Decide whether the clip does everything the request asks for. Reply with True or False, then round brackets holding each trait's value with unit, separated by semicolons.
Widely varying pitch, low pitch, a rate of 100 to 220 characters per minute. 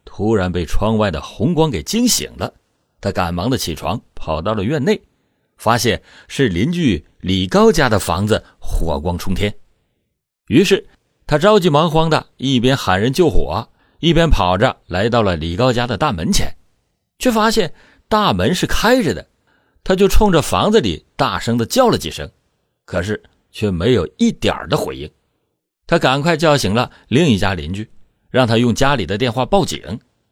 False (7.8 semitones; 115 Hz; 240 characters per minute)